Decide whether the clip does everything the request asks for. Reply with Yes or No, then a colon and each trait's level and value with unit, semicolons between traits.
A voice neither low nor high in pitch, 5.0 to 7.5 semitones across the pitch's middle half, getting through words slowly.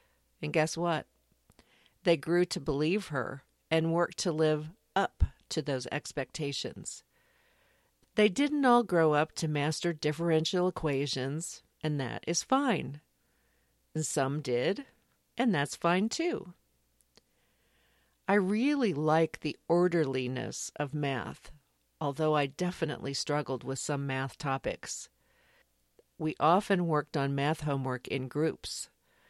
No: medium, 150 Hz; average, 4.3 semitones; slow, 120 wpm